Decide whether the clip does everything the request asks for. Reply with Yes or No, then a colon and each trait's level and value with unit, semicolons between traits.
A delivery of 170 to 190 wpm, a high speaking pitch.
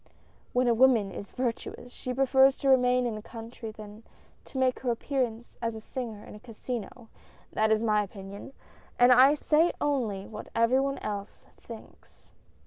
Yes: average, 175 wpm; high, 240 Hz